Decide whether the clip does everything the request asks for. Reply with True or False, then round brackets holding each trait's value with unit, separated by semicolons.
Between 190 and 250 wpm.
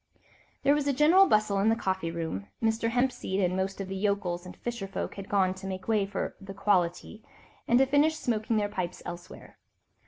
True (195 wpm)